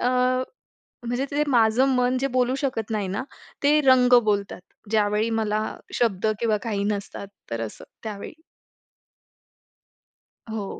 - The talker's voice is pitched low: No, high, 225 Hz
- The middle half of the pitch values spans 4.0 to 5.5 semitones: No, average, 3.3 semitones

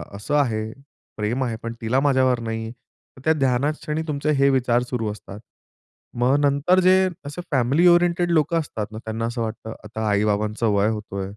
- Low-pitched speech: Yes, low, 125 Hz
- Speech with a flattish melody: No, average, 4.9 semitones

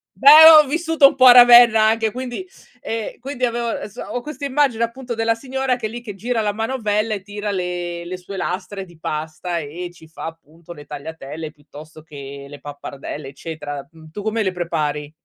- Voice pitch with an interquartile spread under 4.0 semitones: No, wide, 7.1 semitones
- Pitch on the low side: No, high, 205 Hz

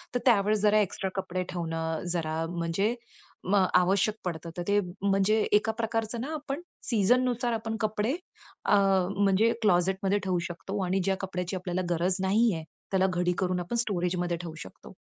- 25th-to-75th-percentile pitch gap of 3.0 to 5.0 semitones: Yes, average, 3.3 semitones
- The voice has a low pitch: No, high, 195 Hz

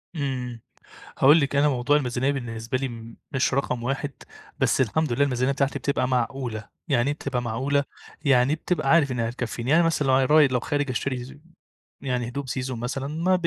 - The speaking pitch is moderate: No, low, 130 Hz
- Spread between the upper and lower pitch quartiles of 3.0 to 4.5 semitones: No, narrow, 2.5 semitones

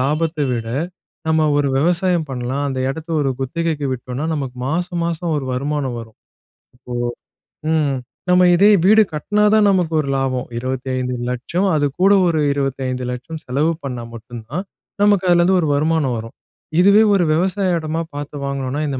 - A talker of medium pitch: Yes, medium, 150 Hz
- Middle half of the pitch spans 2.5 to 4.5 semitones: No, average, 4.9 semitones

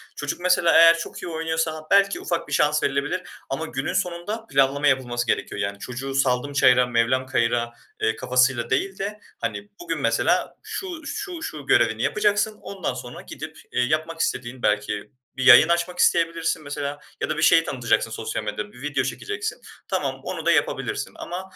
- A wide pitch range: Yes, wide, 6.1 semitones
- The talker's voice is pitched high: No, medium, 150 Hz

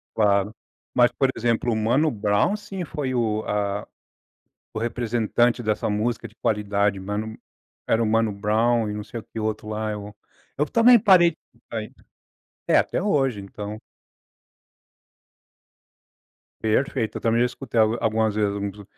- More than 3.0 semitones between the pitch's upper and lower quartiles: No, narrow, 2.5 semitones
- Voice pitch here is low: Yes, low, 110 Hz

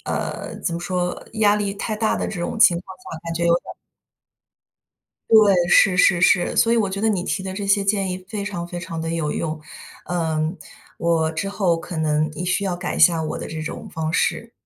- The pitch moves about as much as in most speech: Yes, average, 3.2 semitones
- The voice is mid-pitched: Yes, medium, 180 Hz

